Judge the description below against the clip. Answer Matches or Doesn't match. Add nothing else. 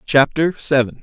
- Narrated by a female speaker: Doesn't match